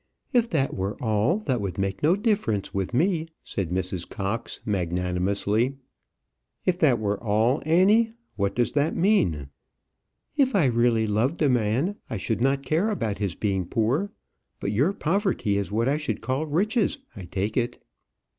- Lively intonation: Yes, wide, 8.3 semitones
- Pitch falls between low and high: No, low, 120 Hz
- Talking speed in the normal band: Yes, average, 165 wpm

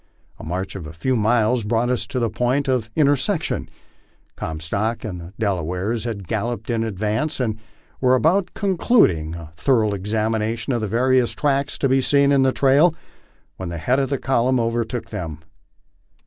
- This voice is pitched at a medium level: No, low, 115 Hz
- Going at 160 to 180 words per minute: Yes, average, 175 wpm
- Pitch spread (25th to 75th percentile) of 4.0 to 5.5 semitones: Yes, average, 4.6 semitones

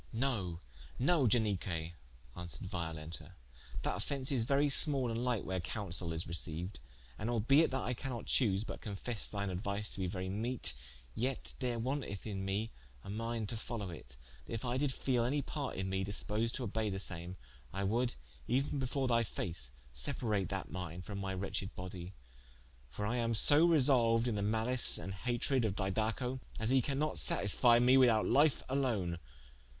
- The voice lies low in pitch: Yes, low, 110 Hz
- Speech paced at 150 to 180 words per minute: Yes, average, 175 wpm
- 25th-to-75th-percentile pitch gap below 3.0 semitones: No, average, 4.8 semitones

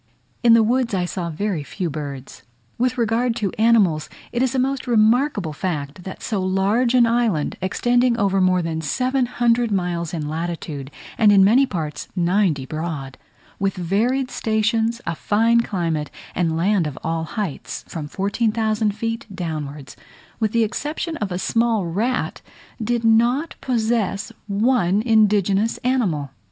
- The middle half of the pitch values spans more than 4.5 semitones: Yes, wide, 5.5 semitones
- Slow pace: No, average, 145 wpm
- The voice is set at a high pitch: Yes, high, 205 Hz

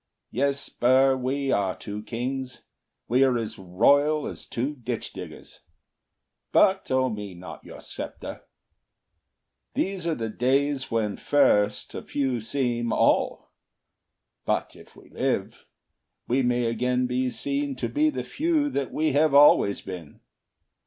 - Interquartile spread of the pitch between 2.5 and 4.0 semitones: Yes, average, 3.6 semitones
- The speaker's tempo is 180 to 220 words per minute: No, average, 140 wpm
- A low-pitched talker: Yes, low, 130 Hz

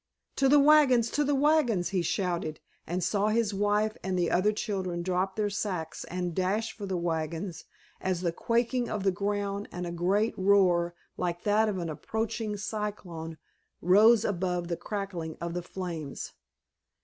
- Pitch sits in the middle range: No, high, 195 Hz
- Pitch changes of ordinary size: Yes, average, 3.5 semitones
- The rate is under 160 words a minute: No, average, 165 wpm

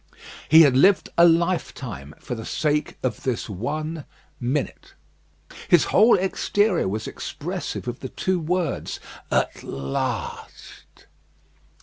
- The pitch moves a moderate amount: No, wide, 6.1 semitones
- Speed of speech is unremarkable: No, slow, 115 wpm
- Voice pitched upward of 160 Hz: No, medium, 150 Hz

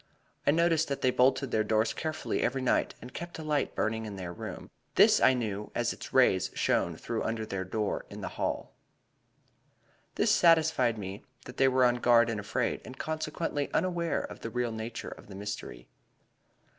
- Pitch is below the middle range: Yes, low, 120 Hz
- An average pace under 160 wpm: No, average, 185 wpm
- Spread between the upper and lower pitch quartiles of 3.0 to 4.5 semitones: No, average, 5.0 semitones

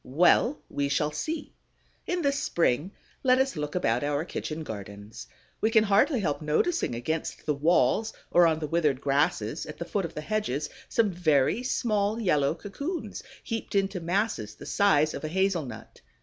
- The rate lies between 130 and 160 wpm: No, average, 175 wpm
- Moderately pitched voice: Yes, medium, 170 Hz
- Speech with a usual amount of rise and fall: No, wide, 6.6 semitones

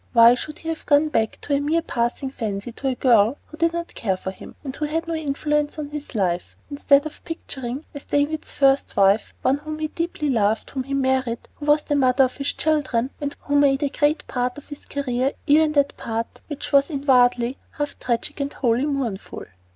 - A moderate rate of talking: No, fast, 215 wpm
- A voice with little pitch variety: No, average, 3.3 semitones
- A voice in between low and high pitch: No, very high, 280 Hz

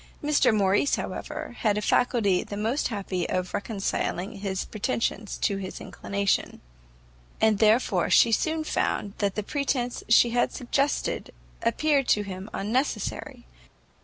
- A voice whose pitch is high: Yes, high, 215 Hz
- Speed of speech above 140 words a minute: No, slow, 135 wpm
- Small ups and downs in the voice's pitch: No, average, 3.6 semitones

